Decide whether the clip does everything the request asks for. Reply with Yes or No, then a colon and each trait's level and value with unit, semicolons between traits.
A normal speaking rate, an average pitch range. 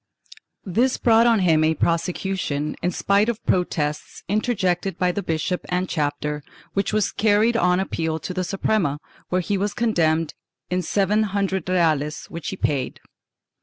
Yes: average, 155 wpm; average, 4.1 semitones